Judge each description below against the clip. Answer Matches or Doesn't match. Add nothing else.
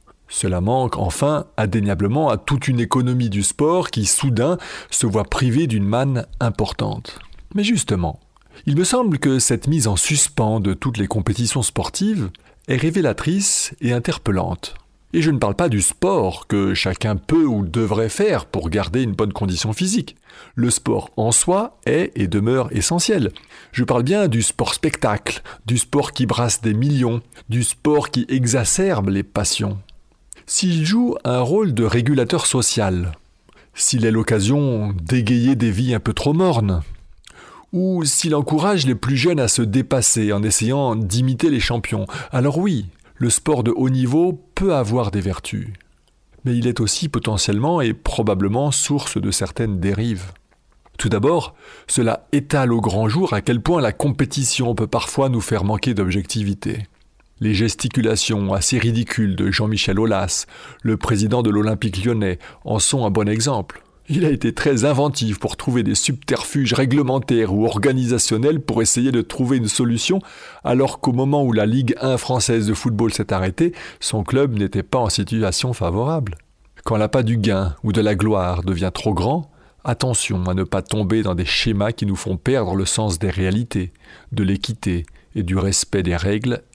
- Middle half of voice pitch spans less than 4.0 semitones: Doesn't match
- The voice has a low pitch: Matches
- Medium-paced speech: Matches